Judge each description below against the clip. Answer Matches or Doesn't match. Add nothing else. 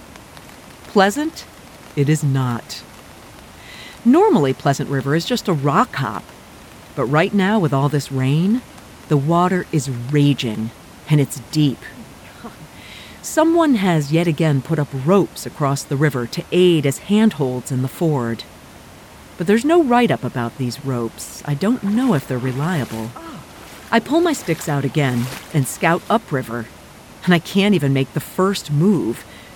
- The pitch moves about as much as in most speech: Doesn't match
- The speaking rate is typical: Matches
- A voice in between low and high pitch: Matches